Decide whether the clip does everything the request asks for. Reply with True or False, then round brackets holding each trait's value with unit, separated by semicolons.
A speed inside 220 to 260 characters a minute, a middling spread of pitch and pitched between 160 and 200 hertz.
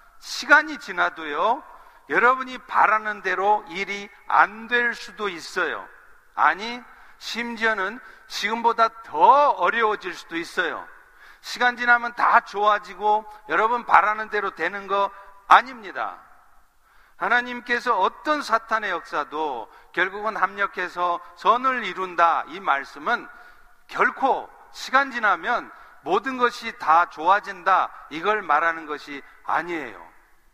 False (250 characters per minute; 4.2 semitones; 215 Hz)